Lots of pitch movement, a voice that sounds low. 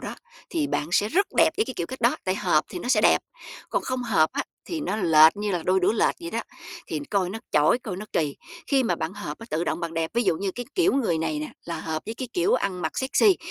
No: wide, 7.0 semitones; high, 200 Hz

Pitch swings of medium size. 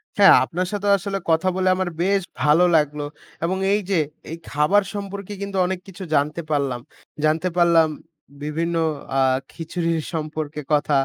Yes: average, 3.8 semitones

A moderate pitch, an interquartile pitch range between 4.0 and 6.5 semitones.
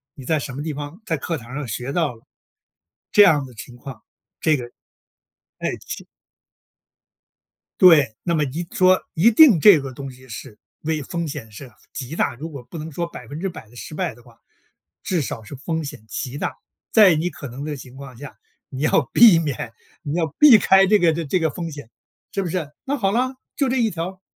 Yes: medium, 155 Hz; average, 5.2 semitones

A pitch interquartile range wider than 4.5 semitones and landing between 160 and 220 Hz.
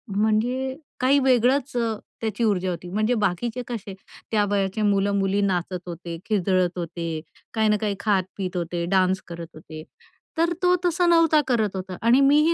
Yes: average, 4.9 semitones; high, 205 Hz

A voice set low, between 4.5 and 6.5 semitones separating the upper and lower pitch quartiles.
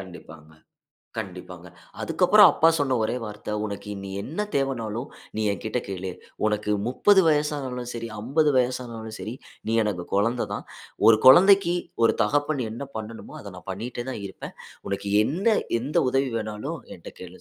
Yes: low, 115 Hz; average, 5.0 semitones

